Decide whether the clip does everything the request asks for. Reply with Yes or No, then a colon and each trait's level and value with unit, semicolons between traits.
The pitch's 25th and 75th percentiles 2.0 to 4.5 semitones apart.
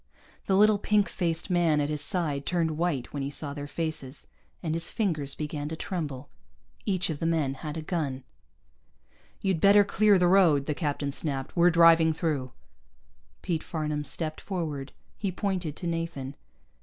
Yes: average, 3.4 semitones